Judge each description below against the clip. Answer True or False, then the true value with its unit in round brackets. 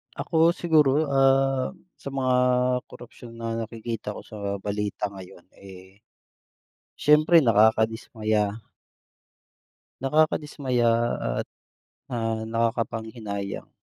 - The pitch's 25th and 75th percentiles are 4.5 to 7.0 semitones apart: False (4.0 semitones)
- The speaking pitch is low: True (115 Hz)